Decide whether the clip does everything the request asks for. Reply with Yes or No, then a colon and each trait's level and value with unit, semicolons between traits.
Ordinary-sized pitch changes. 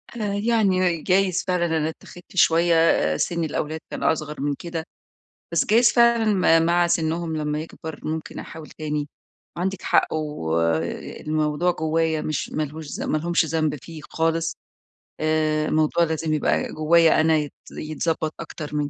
No: narrow, 1.9 semitones